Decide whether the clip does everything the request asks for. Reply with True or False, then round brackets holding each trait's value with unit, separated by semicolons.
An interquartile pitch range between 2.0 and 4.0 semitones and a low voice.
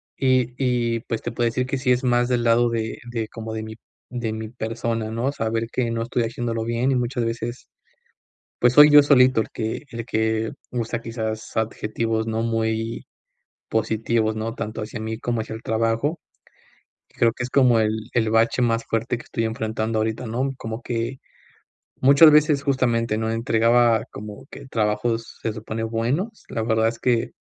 False (1.6 semitones; 115 Hz)